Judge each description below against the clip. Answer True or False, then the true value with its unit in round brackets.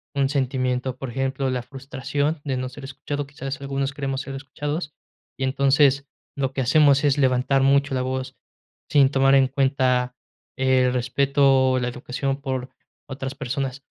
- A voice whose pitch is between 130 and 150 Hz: True (135 Hz)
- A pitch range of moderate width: False (1.1 semitones)